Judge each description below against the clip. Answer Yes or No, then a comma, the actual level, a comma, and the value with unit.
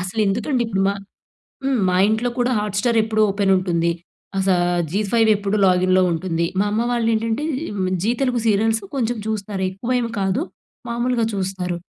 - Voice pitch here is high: Yes, high, 210 Hz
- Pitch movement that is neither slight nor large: Yes, average, 3.6 semitones